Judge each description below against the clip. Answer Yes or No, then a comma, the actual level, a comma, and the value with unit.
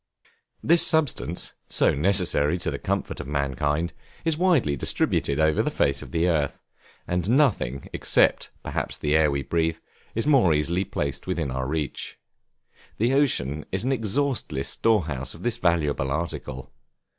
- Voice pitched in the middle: No, very low, 80 Hz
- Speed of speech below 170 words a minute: Yes, average, 155 wpm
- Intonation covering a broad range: Yes, wide, 7.2 semitones